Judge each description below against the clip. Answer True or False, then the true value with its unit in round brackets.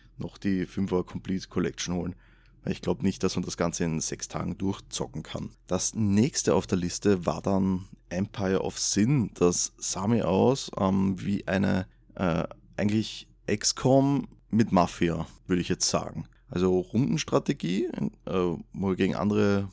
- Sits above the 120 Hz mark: False (95 Hz)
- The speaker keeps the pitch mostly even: True (2.1 semitones)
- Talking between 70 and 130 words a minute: False (155 wpm)